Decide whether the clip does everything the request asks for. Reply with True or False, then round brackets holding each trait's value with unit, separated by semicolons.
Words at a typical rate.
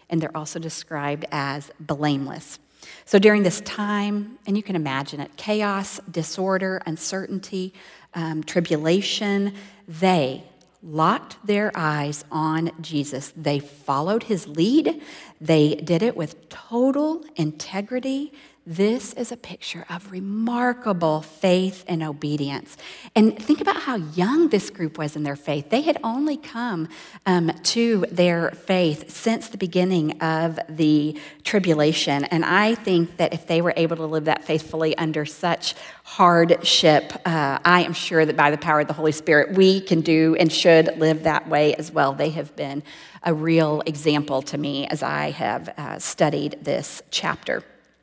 True (150 wpm)